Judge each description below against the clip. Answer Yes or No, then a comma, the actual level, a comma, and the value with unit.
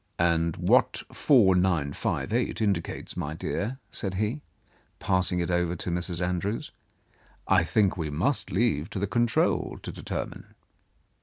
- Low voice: Yes, very low, 90 Hz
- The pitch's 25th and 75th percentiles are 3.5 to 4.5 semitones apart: Yes, average, 3.8 semitones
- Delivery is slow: Yes, slow, 130 wpm